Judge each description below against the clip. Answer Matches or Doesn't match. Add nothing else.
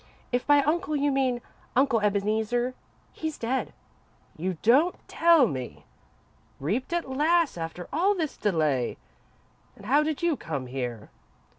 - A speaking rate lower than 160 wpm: Matches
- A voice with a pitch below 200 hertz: Doesn't match